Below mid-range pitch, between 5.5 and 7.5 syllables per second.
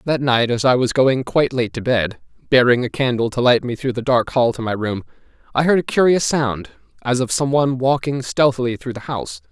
Yes: low, 125 Hz; 5.6 syllables/s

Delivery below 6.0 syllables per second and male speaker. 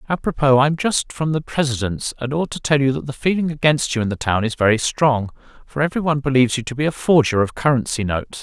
No: 6.4 syllables/s; male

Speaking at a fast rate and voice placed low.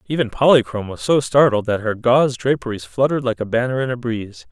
Yes: fast, 215 wpm; low, 120 Hz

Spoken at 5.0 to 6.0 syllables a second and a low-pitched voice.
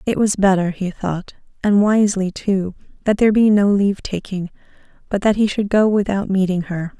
No: 5.3 syllables/s; high, 195 Hz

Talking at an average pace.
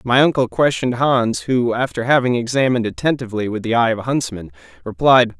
Yes: average, 180 wpm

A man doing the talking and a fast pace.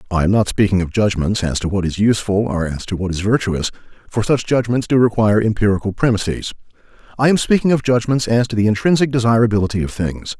Yes: male; fast, 210 wpm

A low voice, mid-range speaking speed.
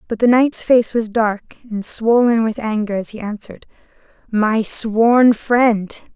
No: high, 225 Hz; average, 155 wpm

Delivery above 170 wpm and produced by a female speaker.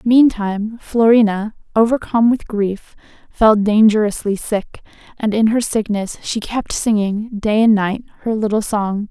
No: average, 140 wpm; female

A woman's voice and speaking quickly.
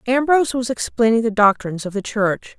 No: female; average, 185 wpm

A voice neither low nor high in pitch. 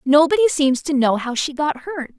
No: very high, 295 Hz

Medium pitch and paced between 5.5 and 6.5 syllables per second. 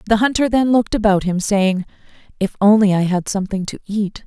No: high, 205 Hz; 5.8 syllables/s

